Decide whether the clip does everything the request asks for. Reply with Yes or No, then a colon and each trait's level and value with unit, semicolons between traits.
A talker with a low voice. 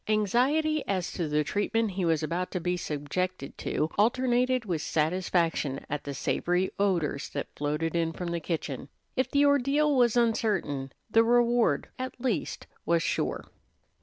No: medium, 185 Hz